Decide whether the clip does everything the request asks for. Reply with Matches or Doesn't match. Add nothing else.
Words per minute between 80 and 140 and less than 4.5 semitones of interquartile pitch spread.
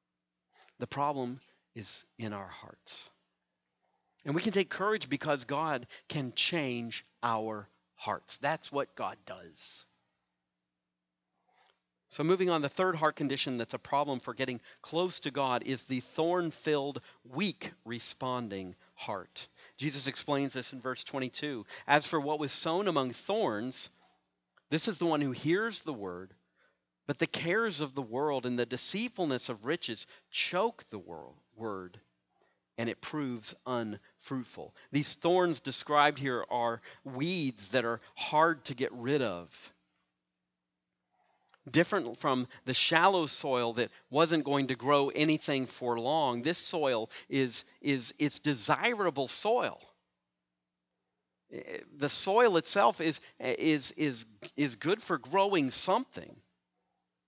Doesn't match